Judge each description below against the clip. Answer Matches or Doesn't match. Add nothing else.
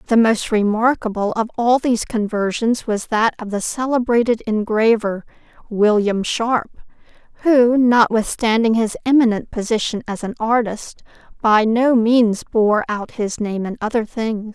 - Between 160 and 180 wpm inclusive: Doesn't match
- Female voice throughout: Matches